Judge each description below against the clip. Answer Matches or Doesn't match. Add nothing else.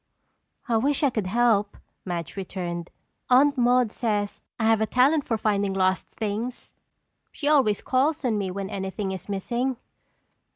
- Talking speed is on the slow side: Doesn't match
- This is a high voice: Matches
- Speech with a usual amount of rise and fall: Matches